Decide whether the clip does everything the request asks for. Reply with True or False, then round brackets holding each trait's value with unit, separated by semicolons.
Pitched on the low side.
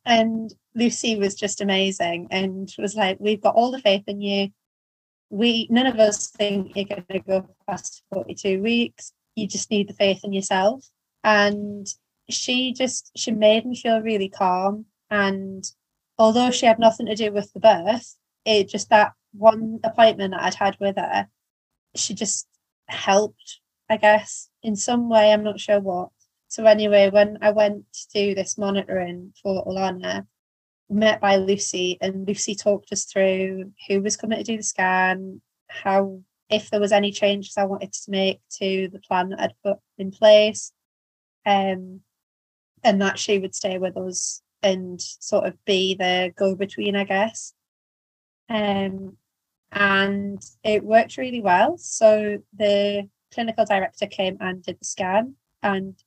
False (200 Hz)